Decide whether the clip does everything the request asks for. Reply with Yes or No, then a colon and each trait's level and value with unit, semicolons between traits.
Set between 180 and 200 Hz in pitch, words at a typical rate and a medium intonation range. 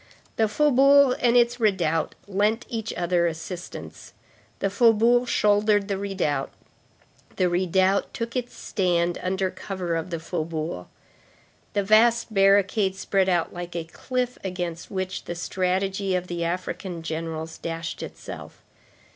No: high, 190 Hz; slow, 130 wpm; average, 3.9 semitones